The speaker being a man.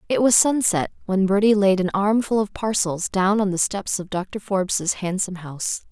No: female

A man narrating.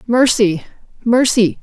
No: female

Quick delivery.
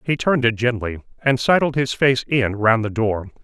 Yes: fast, 210 wpm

